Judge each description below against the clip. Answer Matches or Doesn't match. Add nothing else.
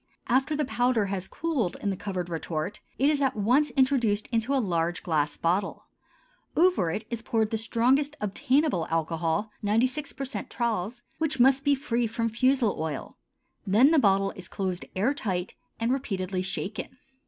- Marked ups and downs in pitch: Matches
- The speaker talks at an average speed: Matches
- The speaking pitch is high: Matches